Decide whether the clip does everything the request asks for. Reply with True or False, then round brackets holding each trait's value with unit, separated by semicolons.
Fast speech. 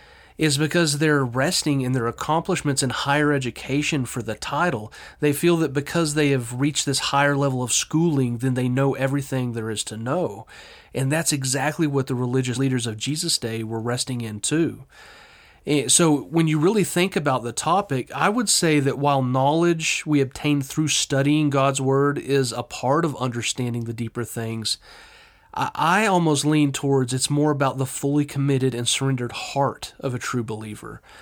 False (180 wpm)